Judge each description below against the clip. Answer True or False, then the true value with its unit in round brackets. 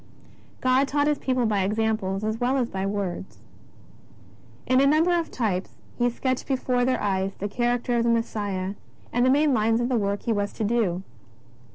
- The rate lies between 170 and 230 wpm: True (190 wpm)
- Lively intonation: False (4.1 semitones)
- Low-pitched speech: False (230 Hz)